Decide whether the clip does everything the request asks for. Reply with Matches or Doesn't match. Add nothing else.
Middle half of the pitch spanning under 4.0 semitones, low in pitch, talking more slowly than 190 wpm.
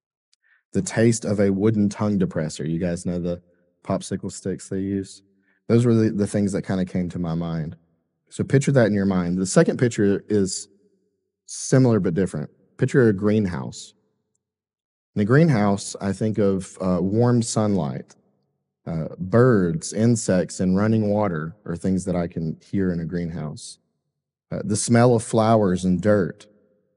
Matches